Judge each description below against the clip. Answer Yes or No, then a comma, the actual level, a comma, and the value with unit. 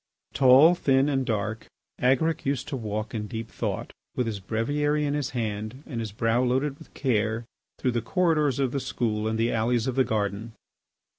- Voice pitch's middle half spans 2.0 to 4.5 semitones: Yes, average, 3.7 semitones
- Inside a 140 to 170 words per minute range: No, average, 190 wpm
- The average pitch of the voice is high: No, low, 120 Hz